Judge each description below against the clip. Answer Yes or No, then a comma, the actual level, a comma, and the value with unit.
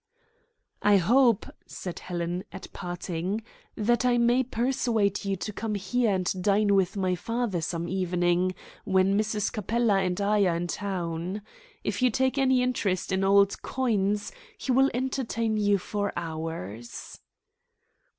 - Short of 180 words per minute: Yes, average, 140 wpm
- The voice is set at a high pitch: Yes, high, 200 Hz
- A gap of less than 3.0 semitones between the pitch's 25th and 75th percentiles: No, average, 4.1 semitones